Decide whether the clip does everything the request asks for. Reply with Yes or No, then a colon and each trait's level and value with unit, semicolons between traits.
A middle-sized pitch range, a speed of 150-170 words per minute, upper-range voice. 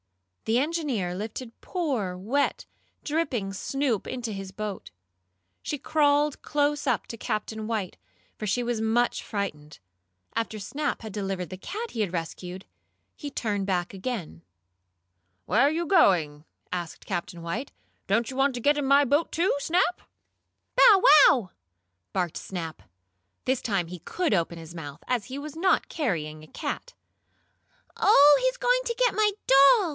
No: wide, 7.6 semitones; average, 155 wpm; high, 230 Hz